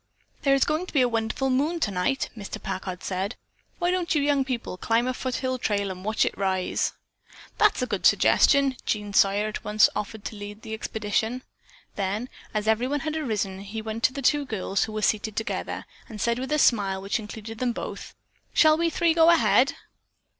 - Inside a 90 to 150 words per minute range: No, average, 195 wpm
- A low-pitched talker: No, high, 225 Hz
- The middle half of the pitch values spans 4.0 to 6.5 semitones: Yes, average, 4.6 semitones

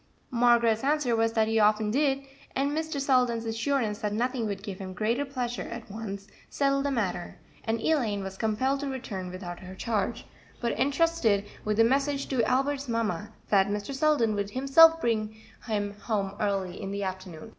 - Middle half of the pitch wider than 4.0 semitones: Yes, average, 4.8 semitones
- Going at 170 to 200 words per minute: Yes, average, 175 wpm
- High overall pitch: Yes, high, 225 Hz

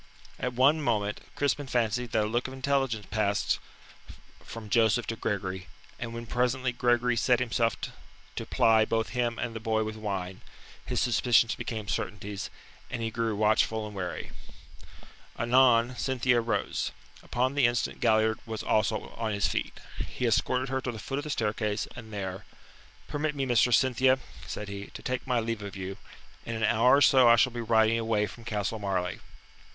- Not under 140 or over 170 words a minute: No, average, 180 wpm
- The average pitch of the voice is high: No, low, 115 Hz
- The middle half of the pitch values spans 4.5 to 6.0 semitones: No, narrow, 2.6 semitones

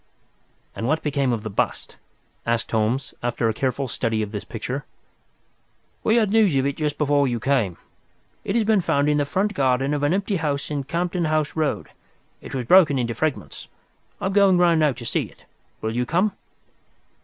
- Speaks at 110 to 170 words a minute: No, average, 195 wpm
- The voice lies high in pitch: No, medium, 145 Hz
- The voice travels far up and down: Yes, wide, 5.7 semitones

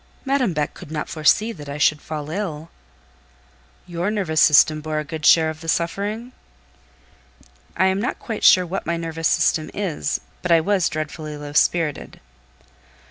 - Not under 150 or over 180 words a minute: Yes, average, 165 wpm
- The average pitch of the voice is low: No, medium, 165 Hz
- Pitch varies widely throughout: No, average, 3.6 semitones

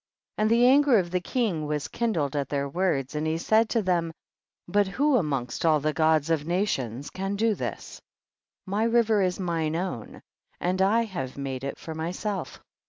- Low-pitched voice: No, medium, 175 Hz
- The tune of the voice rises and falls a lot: Yes, wide, 5.8 semitones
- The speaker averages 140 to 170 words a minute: No, average, 185 wpm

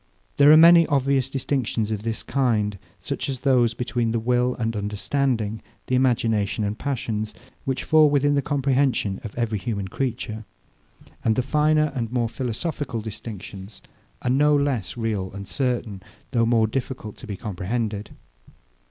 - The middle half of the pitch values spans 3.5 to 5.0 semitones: Yes, average, 3.9 semitones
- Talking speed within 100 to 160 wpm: Yes, average, 150 wpm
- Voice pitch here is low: Yes, low, 120 Hz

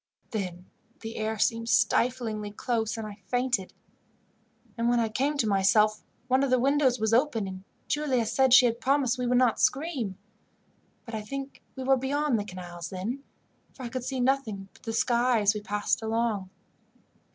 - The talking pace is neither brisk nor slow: Yes, average, 180 wpm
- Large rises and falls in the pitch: No, average, 3.5 semitones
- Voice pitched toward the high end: Yes, high, 235 Hz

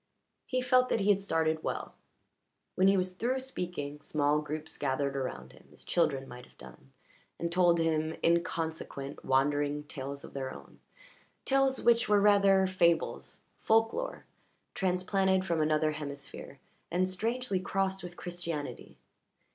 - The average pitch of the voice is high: No, medium, 170 Hz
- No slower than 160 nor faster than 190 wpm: No, average, 140 wpm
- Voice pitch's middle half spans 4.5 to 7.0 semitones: Yes, average, 4.8 semitones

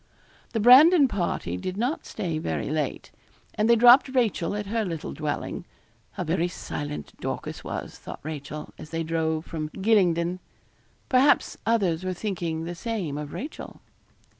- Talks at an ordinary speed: Yes, average, 150 wpm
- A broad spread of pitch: Yes, wide, 6.1 semitones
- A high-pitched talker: No, medium, 180 Hz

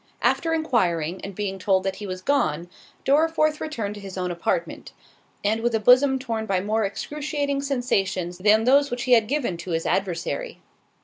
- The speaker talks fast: No, average, 180 wpm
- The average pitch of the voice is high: Yes, high, 220 Hz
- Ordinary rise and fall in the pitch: No, wide, 6.7 semitones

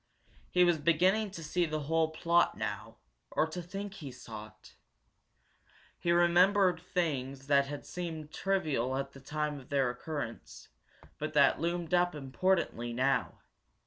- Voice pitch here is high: No, medium, 155 Hz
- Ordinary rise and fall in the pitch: Yes, average, 4.2 semitones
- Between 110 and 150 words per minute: Yes, average, 145 wpm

